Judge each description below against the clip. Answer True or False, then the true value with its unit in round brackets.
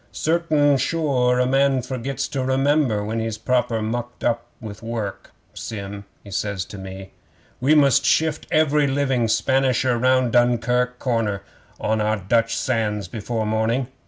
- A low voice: True (120 Hz)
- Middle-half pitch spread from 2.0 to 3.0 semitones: False (3.5 semitones)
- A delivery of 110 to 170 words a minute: True (150 wpm)